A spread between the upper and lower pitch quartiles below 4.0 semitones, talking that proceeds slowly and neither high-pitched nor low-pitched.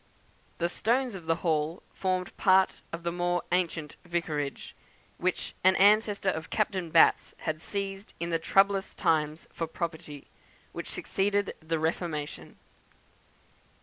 Yes: average, 3.1 semitones; slow, 130 wpm; medium, 175 Hz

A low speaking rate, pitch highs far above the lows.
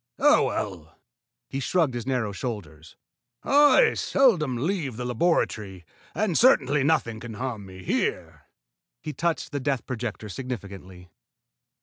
Yes: slow, 125 wpm; wide, 6.7 semitones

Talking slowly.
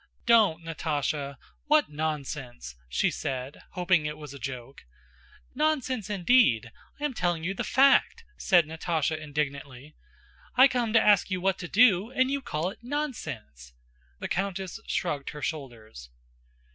No: average, 145 wpm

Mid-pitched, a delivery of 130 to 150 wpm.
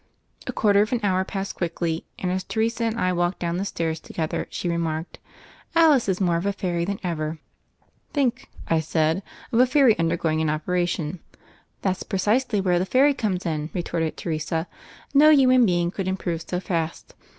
No: medium, 180 Hz; average, 185 wpm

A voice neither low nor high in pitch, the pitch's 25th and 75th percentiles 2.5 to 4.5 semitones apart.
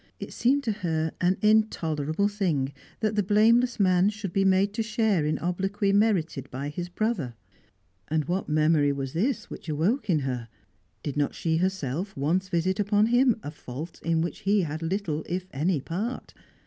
No: medium, 180 Hz; average, 5.0 semitones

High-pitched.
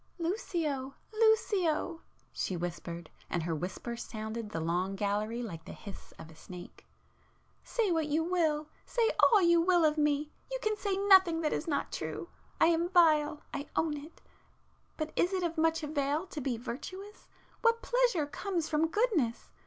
Yes: very high, 310 Hz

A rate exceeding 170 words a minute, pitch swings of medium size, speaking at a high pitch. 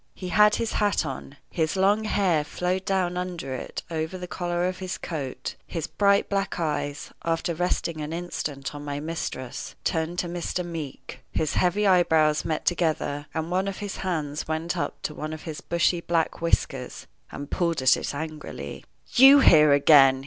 No: average, 180 wpm; average, 3.2 semitones; medium, 165 Hz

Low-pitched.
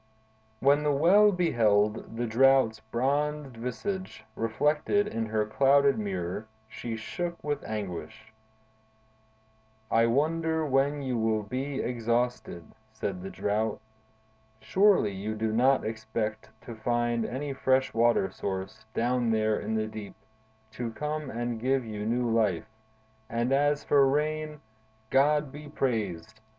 Yes: low, 120 Hz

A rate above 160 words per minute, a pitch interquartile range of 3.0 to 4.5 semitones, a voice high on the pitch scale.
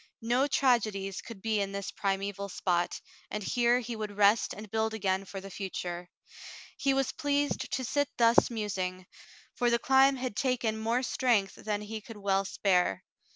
Yes: average, 170 wpm; average, 3.6 semitones; high, 215 Hz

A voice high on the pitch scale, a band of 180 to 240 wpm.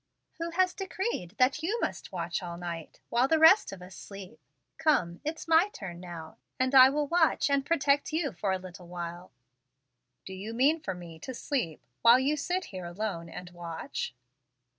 Yes: high, 220 Hz; average, 185 wpm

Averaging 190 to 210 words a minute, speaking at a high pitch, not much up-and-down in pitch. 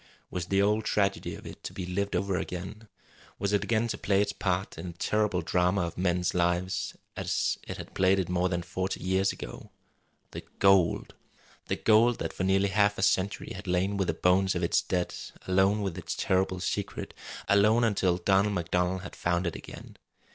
No: average, 195 wpm; very low, 95 Hz; narrow, 1.9 semitones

